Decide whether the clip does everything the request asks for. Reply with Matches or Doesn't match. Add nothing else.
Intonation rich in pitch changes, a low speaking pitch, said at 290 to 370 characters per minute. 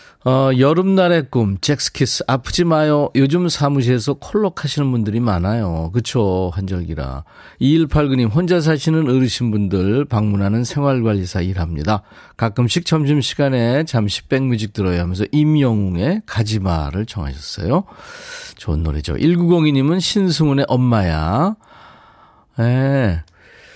Doesn't match